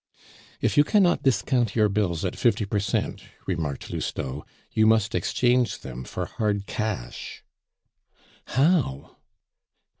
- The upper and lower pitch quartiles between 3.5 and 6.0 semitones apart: Yes, average, 5.1 semitones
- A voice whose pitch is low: Yes, low, 105 Hz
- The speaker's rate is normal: No, slow, 120 wpm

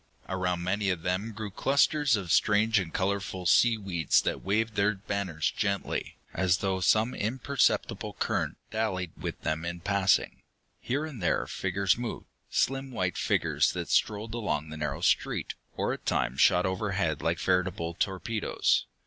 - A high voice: No, low, 100 Hz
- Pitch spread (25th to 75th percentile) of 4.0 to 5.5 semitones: No, average, 3.4 semitones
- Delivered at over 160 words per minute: No, average, 150 wpm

